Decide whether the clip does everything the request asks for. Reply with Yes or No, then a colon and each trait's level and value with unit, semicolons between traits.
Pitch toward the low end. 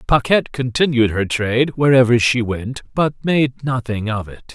Yes: low, 125 Hz